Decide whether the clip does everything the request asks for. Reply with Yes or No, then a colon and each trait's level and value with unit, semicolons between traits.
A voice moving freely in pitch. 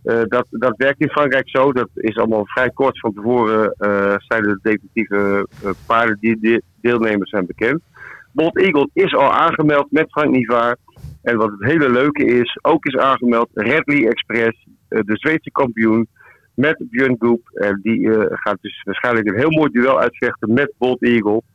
No: average, 3.3 semitones